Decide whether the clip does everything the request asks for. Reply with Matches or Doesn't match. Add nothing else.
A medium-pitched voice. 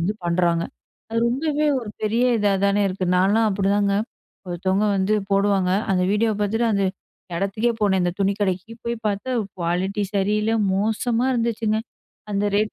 Doesn't match